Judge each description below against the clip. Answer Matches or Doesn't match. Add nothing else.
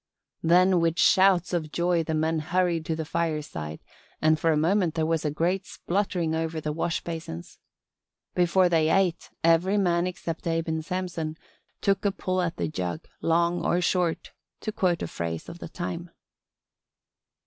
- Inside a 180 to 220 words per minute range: Doesn't match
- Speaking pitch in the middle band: Matches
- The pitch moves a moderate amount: Doesn't match